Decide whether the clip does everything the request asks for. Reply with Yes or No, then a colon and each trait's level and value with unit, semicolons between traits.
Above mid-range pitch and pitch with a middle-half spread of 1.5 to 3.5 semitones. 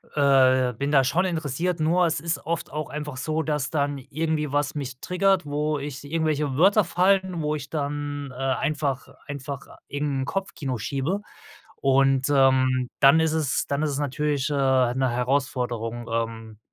No: medium, 145 Hz; average, 2.8 semitones